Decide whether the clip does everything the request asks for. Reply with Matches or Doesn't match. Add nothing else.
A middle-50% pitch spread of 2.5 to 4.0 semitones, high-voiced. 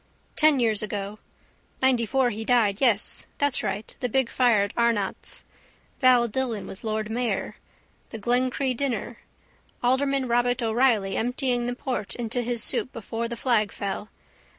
Matches